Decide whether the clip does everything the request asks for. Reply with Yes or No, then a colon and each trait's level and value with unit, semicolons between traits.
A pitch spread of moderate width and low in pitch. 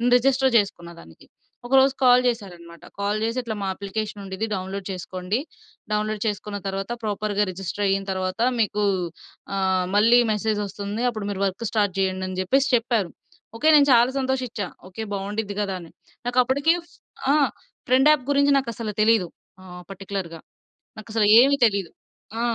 No: average, 3.7 semitones; high, 210 Hz